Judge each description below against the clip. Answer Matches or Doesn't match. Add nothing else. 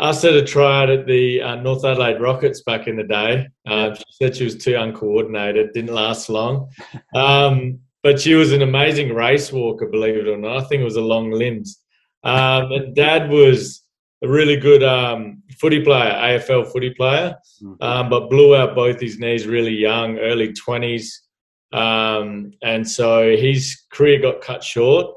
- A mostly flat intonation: Doesn't match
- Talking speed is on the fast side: Doesn't match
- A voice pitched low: Matches